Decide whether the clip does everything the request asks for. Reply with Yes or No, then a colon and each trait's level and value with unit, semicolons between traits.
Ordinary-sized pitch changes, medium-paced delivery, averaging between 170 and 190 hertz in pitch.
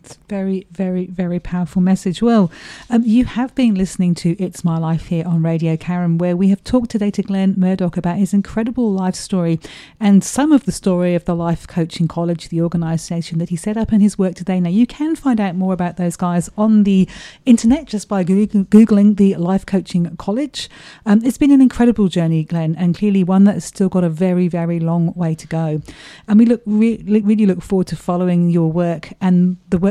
No: average, 3.3 semitones; fast, 215 wpm; medium, 185 Hz